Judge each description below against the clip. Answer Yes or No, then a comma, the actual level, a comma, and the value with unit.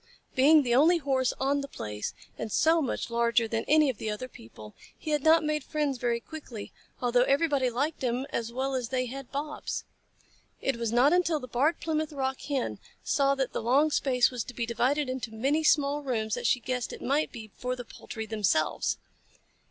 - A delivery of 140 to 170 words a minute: No, average, 200 wpm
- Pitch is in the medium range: No, very high, 260 Hz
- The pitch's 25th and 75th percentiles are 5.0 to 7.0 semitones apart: No, average, 3.7 semitones